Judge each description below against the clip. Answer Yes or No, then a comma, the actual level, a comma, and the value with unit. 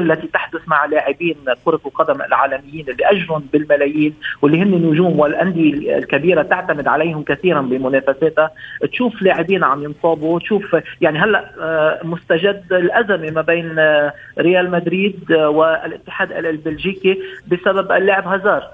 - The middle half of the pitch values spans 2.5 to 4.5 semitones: Yes, average, 3.5 semitones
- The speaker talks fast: No, average, 115 wpm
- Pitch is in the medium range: Yes, medium, 160 Hz